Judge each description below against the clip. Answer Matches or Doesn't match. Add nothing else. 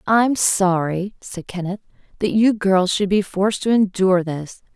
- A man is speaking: Doesn't match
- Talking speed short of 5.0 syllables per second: Matches